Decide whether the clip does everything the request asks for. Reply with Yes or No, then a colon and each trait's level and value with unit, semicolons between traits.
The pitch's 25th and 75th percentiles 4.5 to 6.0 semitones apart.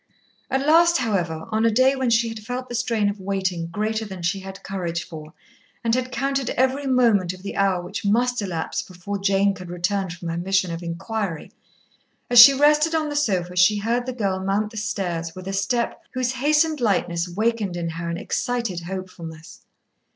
Yes: wide, 5.4 semitones